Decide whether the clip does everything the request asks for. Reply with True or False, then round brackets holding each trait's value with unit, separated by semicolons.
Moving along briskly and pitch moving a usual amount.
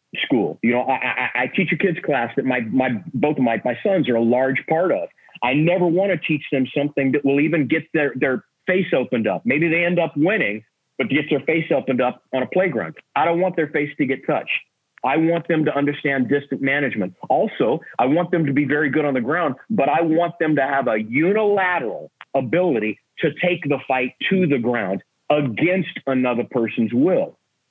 True (215 wpm; 4.5 semitones)